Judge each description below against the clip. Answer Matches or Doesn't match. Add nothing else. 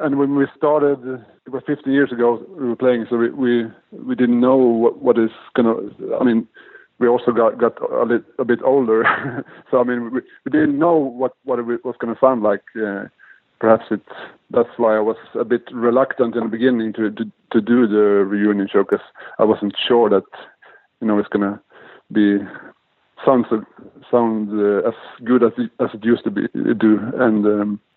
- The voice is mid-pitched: Doesn't match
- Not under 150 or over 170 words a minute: Doesn't match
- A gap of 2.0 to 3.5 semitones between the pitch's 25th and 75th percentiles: Matches